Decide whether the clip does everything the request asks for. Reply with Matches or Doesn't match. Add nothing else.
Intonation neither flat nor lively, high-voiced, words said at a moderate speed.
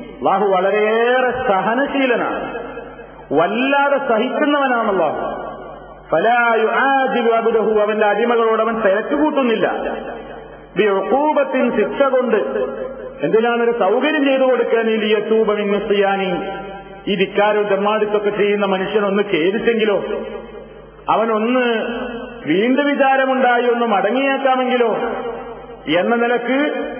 Matches